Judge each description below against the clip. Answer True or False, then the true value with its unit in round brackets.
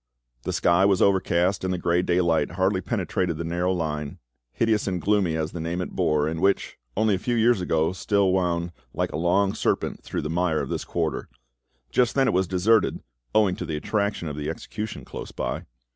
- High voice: False (90 Hz)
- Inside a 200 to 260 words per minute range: True (205 wpm)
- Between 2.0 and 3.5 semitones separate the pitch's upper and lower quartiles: True (3.0 semitones)